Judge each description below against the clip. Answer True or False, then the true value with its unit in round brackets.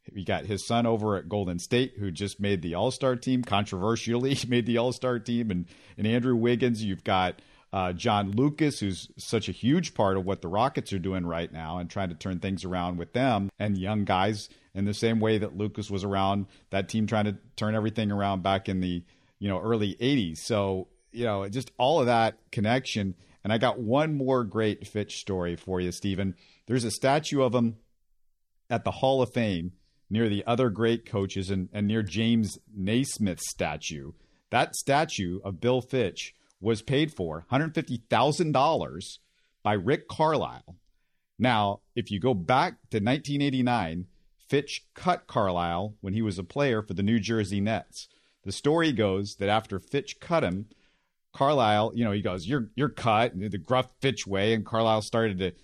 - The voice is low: True (105 Hz)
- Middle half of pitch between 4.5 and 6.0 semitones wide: False (4.0 semitones)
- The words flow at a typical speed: True (185 wpm)